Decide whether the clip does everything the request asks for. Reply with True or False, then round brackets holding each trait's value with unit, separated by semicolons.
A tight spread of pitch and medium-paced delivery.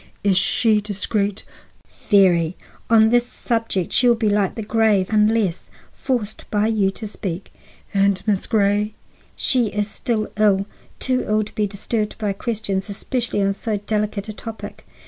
True (2.0 semitones; 155 wpm)